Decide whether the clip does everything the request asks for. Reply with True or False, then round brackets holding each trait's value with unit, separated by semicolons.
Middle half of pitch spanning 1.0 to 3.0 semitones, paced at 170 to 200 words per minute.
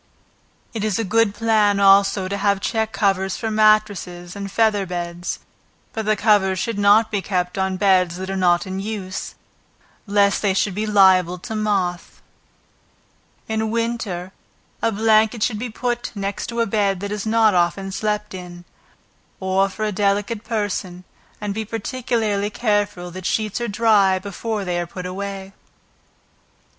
False (2.4 semitones; 155 wpm)